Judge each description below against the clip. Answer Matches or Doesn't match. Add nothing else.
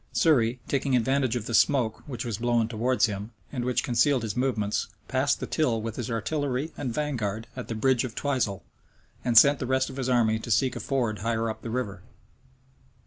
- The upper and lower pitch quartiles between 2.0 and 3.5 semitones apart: Matches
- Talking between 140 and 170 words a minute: Doesn't match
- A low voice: Matches